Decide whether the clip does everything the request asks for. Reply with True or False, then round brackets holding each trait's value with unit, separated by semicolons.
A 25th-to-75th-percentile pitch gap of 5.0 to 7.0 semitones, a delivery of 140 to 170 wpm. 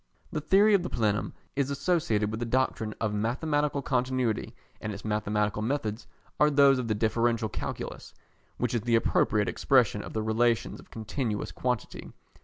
False (4.1 semitones; 165 wpm)